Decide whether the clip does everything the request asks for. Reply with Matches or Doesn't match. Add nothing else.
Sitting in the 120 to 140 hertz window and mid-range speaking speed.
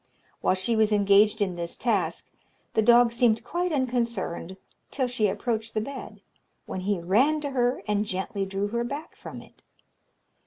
Doesn't match